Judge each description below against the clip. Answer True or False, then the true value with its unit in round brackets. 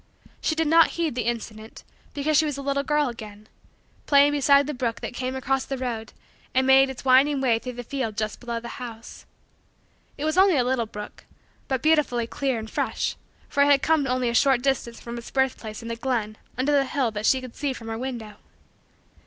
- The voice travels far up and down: False (3.2 semitones)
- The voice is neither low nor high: False (260 Hz)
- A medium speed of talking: False (220 wpm)